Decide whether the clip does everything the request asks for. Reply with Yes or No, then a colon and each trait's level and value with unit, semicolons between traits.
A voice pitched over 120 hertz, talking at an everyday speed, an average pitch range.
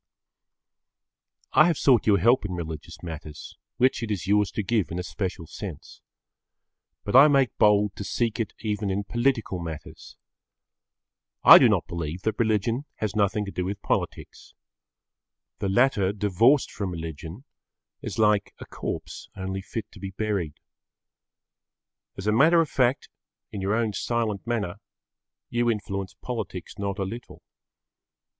No: low, 105 Hz; average, 150 wpm; average, 3.5 semitones